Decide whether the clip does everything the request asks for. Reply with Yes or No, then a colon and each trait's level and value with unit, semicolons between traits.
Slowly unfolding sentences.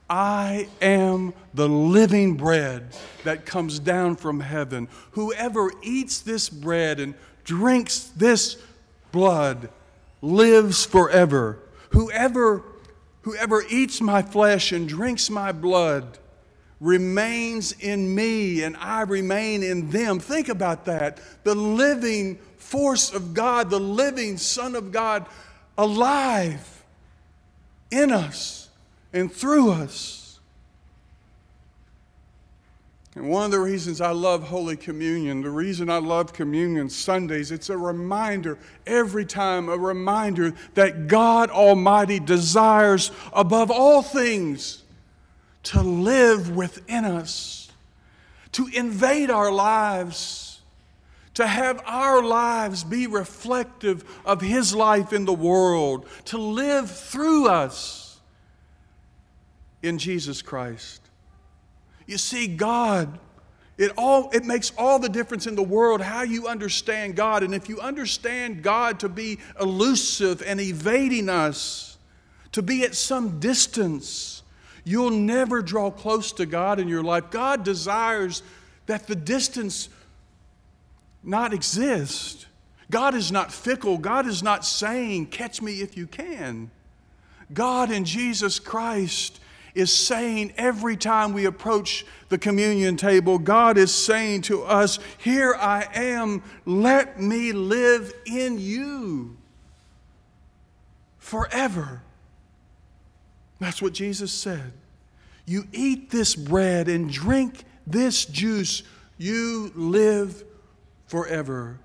Yes: slow, 115 wpm